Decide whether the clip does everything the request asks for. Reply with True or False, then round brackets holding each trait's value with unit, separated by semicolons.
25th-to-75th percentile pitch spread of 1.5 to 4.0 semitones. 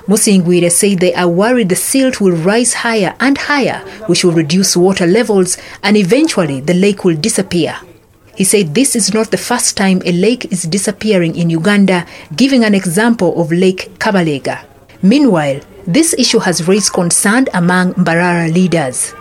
True (3.7 semitones)